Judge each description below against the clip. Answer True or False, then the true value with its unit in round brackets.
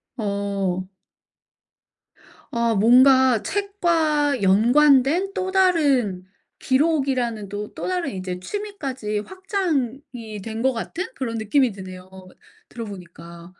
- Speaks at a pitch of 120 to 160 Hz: False (245 Hz)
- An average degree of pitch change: False (6.7 semitones)